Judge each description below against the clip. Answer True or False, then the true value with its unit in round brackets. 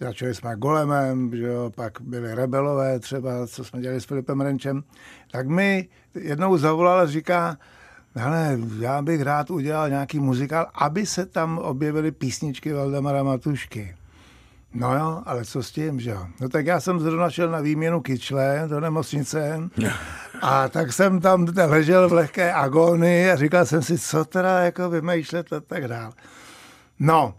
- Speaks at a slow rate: False (160 wpm)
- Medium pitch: True (145 Hz)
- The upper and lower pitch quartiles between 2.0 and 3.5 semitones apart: False (4.4 semitones)